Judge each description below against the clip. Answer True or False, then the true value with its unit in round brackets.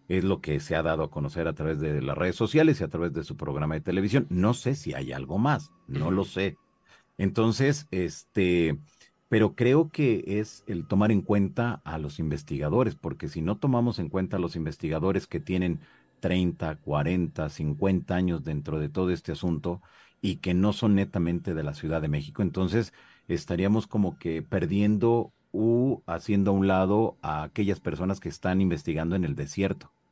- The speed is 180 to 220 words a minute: True (185 wpm)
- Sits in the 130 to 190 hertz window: False (95 Hz)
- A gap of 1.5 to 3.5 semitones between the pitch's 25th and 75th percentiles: False (4.2 semitones)